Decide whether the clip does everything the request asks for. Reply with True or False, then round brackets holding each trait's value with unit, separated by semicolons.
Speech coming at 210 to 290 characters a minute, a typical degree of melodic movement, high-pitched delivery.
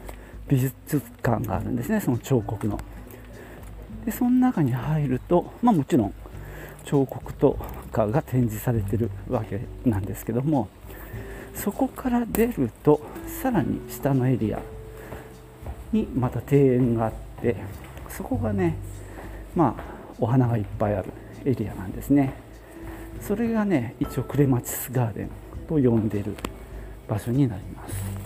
False (260 characters per minute; 4.8 semitones; 120 Hz)